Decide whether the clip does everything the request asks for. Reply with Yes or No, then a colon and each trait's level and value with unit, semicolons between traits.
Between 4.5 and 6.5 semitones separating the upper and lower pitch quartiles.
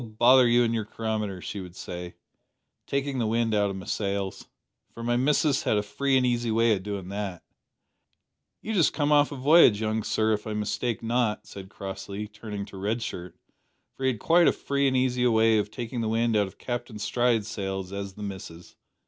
No: average, 3.4 semitones